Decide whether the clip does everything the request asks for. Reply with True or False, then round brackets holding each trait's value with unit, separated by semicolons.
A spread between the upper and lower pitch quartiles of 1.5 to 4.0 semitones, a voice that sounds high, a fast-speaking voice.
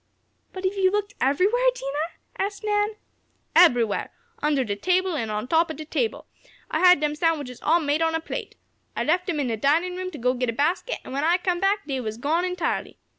False (5.0 semitones; 325 Hz; 225 wpm)